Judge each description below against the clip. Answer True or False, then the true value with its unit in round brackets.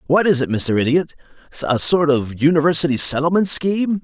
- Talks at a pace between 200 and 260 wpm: False (150 wpm)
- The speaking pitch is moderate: True (150 Hz)